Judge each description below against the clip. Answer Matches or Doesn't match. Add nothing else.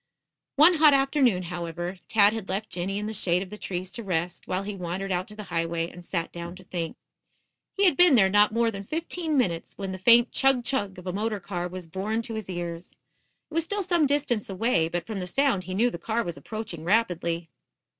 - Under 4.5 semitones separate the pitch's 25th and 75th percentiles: Doesn't match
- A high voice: Matches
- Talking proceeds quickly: Matches